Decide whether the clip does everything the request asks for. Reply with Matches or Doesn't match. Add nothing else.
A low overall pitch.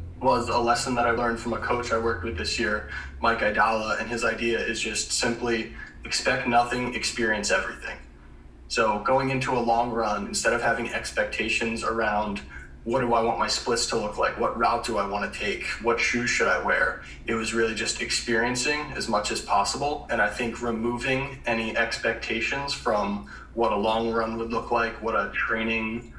Matches